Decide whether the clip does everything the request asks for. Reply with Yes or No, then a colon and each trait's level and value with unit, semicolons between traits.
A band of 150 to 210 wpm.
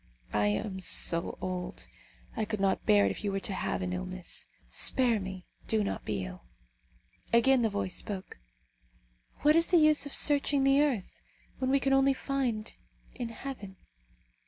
Yes: average, 170 wpm